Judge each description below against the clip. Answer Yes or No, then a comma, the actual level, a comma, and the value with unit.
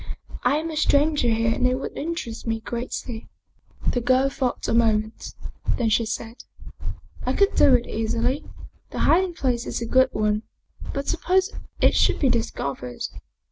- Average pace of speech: Yes, average, 170 wpm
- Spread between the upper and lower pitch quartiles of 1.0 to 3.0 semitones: No, average, 3.8 semitones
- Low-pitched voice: No, high, 245 Hz